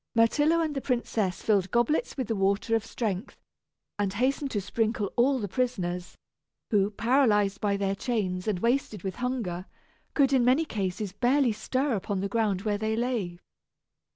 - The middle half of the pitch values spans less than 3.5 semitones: No, average, 4.2 semitones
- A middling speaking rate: Yes, average, 165 wpm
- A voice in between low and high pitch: No, high, 220 Hz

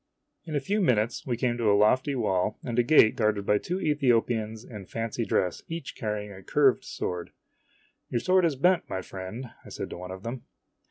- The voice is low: Yes, low, 115 Hz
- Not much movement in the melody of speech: No, average, 4.3 semitones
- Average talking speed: No, fast, 210 wpm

